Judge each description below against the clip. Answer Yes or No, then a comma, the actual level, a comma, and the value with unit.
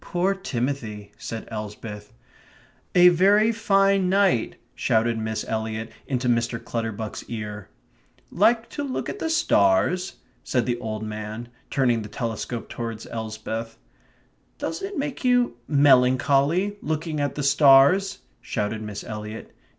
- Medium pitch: No, low, 125 Hz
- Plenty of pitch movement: Yes, wide, 8.6 semitones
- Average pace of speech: No, slow, 125 wpm